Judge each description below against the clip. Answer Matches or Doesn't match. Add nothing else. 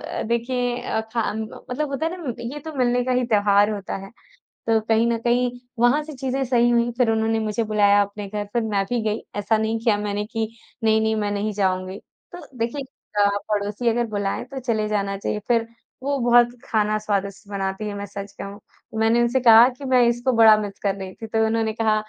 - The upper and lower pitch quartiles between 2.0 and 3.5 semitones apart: Matches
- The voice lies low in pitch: Doesn't match